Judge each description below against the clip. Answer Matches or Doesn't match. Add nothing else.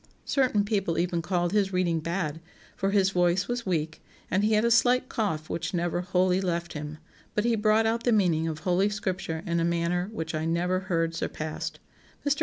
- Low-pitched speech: Doesn't match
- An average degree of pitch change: Matches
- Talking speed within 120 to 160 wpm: Doesn't match